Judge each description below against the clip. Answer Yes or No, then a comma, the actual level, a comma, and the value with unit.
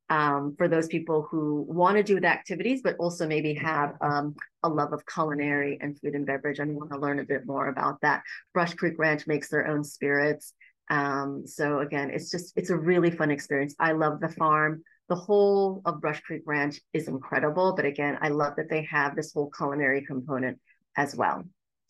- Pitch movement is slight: Yes, narrow, 2.2 semitones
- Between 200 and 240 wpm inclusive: Yes, fast, 205 wpm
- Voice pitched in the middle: Yes, medium, 150 Hz